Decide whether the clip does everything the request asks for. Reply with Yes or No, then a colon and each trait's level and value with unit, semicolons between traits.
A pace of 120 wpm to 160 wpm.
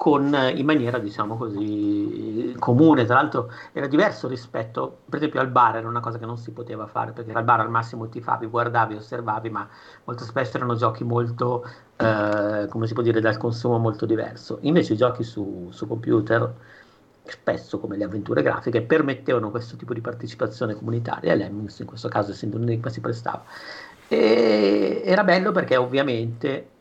No: fast, 170 wpm